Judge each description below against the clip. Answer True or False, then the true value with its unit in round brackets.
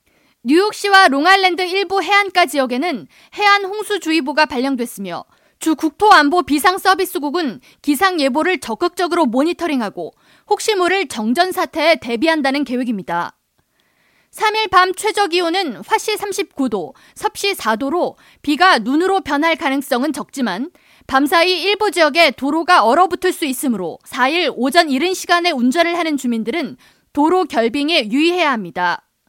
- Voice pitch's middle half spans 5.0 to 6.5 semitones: True (5.4 semitones)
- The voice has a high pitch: True (330 Hz)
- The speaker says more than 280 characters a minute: True (315 characters per minute)